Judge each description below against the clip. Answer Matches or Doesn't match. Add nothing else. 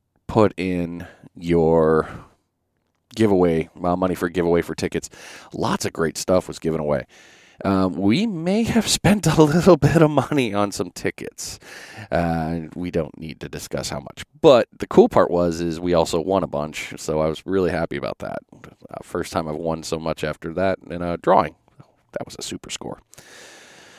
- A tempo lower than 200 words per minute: Matches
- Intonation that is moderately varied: Matches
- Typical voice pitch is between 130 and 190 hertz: Doesn't match